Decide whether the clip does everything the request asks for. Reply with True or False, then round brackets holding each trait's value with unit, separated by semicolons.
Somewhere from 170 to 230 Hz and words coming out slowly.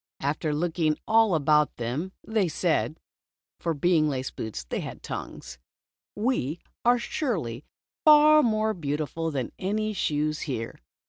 False (160 Hz; 130 wpm)